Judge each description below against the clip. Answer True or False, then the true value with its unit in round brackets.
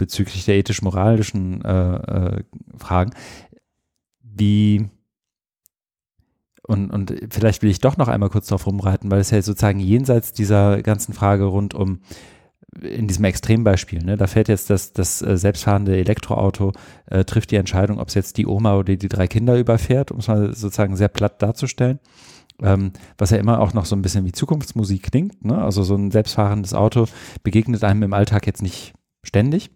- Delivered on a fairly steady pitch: True (1.9 semitones)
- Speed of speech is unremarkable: True (170 wpm)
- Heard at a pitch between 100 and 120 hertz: True (105 Hz)